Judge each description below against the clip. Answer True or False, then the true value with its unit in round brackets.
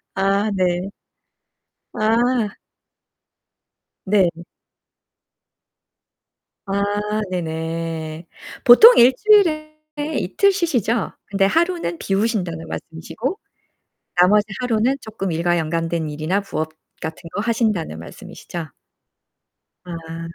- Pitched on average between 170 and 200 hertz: True (195 Hz)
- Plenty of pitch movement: True (5.9 semitones)